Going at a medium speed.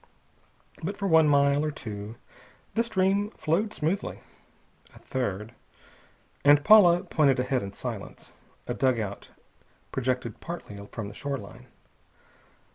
No: slow, 120 wpm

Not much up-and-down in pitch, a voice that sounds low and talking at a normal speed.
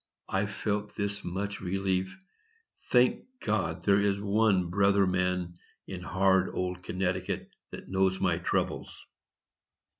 No: narrow, 1.9 semitones; very low, 95 Hz; slow, 115 wpm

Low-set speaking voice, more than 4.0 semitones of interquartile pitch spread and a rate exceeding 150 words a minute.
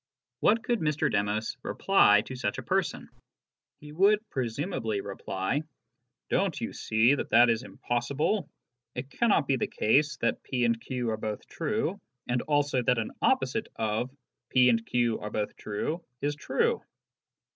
Yes: low, 125 Hz; average, 5.2 semitones; average, 165 wpm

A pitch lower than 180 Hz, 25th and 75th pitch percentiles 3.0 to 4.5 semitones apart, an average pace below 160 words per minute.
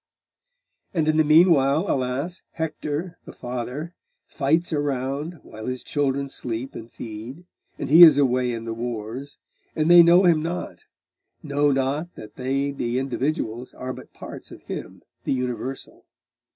Yes: medium, 140 Hz; average, 3.7 semitones; average, 150 wpm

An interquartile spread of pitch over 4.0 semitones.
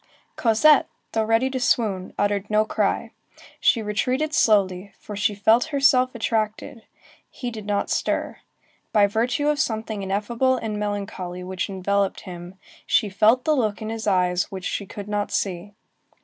No: average, 2.8 semitones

